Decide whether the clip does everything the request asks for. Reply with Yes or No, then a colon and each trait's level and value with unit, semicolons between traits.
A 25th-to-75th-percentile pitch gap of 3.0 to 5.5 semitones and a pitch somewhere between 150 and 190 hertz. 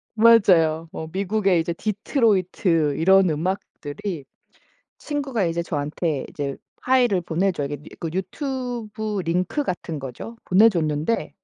Yes: average, 5.1 semitones; medium, 185 Hz